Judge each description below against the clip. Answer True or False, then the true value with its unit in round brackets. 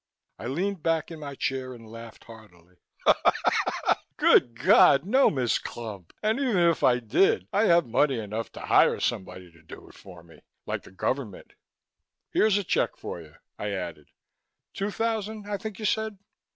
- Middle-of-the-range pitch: False (130 Hz)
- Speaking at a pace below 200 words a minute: True (170 wpm)